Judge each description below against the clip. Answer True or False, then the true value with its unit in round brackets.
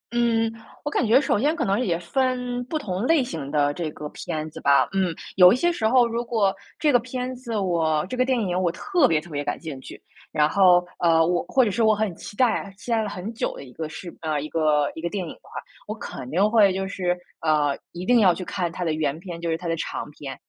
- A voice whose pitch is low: False (185 Hz)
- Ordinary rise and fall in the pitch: False (6.5 semitones)